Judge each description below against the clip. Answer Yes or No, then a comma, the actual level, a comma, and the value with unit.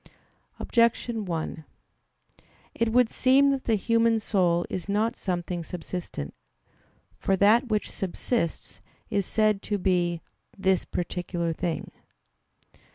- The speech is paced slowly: Yes, slow, 110 wpm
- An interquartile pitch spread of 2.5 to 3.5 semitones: No, average, 4.7 semitones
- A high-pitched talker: Yes, high, 200 Hz